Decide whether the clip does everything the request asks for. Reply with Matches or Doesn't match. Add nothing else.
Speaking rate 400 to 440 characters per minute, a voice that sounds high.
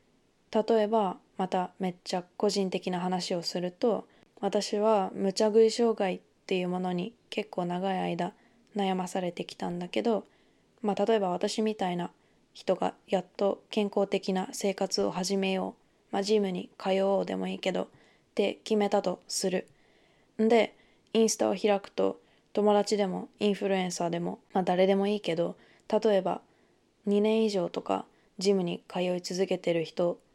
Doesn't match